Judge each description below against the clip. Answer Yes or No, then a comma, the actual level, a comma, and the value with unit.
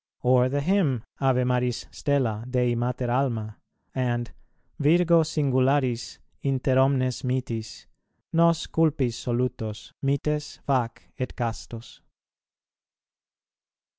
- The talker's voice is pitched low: Yes, low, 130 Hz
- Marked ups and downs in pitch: No, average, 2.8 semitones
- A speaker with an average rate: No, slow, 95 wpm